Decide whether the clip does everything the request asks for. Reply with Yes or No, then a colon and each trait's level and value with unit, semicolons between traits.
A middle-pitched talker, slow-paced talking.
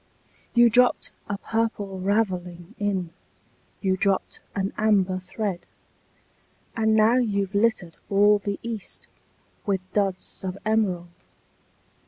No: high, 200 Hz; slow, 110 wpm